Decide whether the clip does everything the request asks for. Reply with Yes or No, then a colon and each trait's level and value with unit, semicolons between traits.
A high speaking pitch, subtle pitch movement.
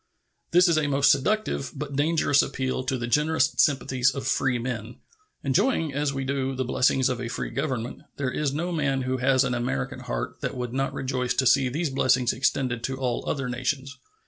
No: low, 135 Hz; narrow, 2.1 semitones